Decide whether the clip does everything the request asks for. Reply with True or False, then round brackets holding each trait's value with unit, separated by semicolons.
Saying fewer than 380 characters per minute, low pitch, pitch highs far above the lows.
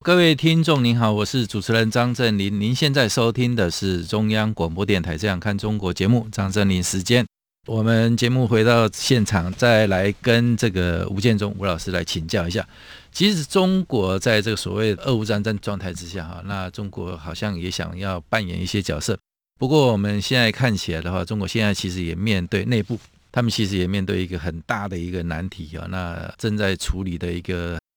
False (305 characters per minute; 100 Hz; 4.1 semitones)